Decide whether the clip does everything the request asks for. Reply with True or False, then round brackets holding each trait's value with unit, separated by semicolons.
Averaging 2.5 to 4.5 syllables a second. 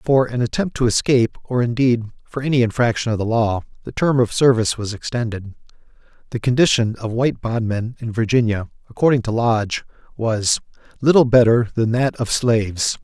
False (5.5 syllables/s)